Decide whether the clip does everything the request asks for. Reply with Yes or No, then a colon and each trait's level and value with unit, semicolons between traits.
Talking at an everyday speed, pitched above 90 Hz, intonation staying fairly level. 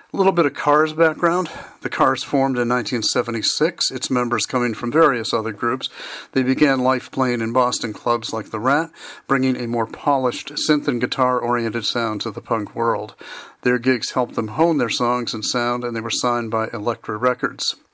Yes: average, 190 wpm; low, 125 Hz; narrow, 2.2 semitones